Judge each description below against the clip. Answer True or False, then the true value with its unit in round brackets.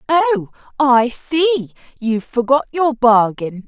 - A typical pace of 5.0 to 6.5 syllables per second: False (3.9 syllables/s)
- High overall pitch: True (260 Hz)